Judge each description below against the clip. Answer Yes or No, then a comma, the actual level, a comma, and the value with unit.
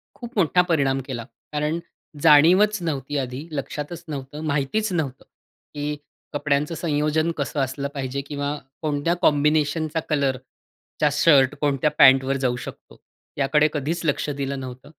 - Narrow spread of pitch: Yes, narrow, 2.3 semitones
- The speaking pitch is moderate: Yes, medium, 145 Hz